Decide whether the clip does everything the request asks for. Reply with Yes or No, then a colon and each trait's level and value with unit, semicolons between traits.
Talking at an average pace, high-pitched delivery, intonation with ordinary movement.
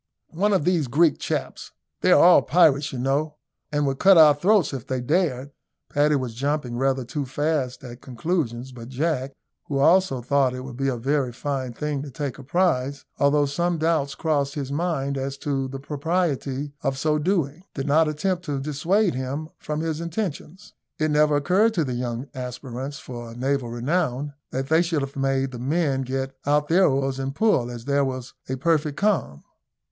No: average, 190 wpm; medium, 140 Hz; average, 3.2 semitones